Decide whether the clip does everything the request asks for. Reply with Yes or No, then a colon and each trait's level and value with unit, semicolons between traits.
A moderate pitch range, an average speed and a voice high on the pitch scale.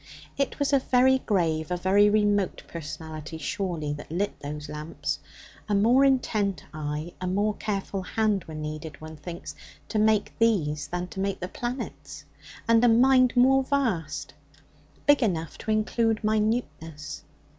No: wide, 6.2 semitones; average, 150 wpm; high, 200 Hz